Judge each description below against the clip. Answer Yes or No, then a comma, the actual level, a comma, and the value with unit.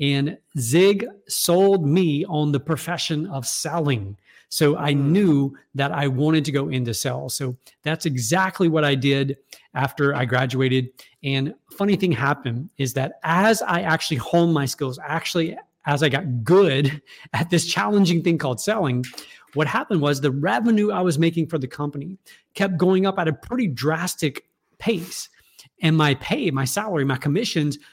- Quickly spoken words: No, average, 165 wpm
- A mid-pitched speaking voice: Yes, medium, 150 Hz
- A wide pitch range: No, average, 3.8 semitones